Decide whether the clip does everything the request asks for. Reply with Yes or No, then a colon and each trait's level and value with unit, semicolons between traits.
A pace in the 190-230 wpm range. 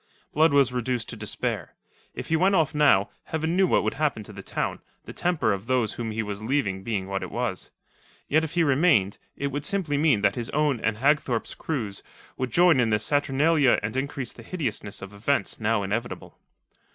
Yes: average, 200 wpm